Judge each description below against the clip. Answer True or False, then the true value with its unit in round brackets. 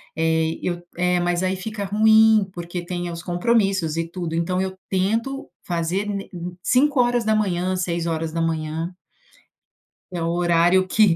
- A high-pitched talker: False (180 Hz)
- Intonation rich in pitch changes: False (3.1 semitones)